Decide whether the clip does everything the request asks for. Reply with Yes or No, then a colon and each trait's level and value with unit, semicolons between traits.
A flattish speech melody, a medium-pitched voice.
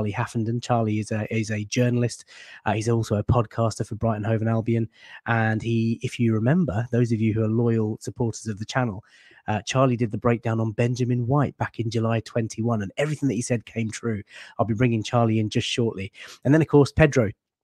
No: narrow, 1.7 semitones; low, 115 Hz